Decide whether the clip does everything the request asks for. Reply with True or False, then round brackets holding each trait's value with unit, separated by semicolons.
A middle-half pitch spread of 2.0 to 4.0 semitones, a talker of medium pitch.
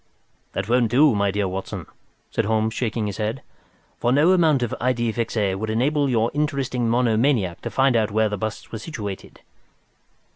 False (3.3 semitones; 115 Hz)